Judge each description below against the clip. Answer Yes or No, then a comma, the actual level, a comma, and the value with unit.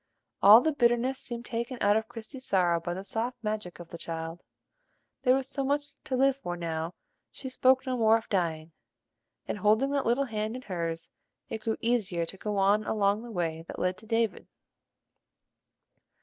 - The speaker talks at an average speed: Yes, average, 185 wpm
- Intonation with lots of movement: Yes, wide, 5.7 semitones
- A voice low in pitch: No, high, 220 Hz